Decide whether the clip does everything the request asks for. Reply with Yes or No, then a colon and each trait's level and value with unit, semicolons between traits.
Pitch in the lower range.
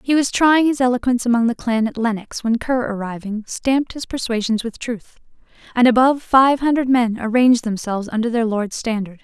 No: high, 235 Hz